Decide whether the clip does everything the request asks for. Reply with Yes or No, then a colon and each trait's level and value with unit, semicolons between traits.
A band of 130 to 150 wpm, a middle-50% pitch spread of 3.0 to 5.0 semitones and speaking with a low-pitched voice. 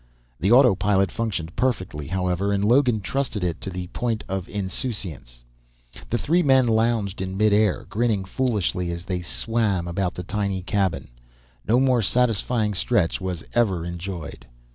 Yes: average, 145 wpm; average, 4.3 semitones; low, 100 Hz